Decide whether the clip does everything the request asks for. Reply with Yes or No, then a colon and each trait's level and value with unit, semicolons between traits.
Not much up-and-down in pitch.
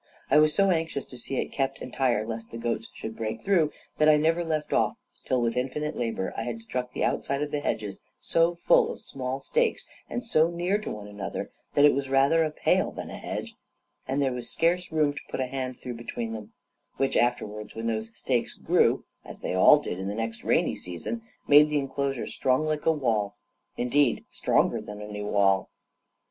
No: average, 5.0 semitones